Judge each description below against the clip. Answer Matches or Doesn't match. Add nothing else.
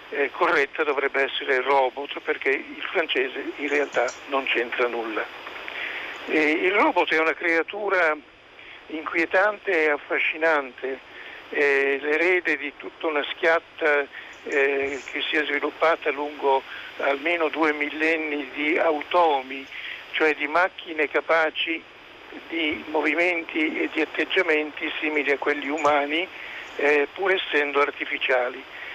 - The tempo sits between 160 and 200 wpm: Doesn't match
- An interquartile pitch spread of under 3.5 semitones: Matches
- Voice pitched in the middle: Matches